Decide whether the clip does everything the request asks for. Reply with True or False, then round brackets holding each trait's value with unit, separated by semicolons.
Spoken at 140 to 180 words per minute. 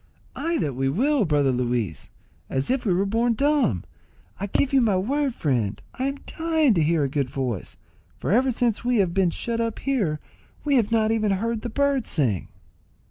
False (195 wpm)